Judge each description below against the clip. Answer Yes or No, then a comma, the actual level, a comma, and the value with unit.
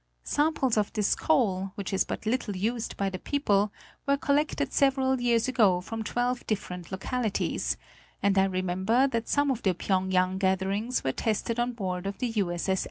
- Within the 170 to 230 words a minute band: Yes, average, 180 wpm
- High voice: Yes, high, 215 Hz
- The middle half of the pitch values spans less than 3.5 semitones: No, average, 4.7 semitones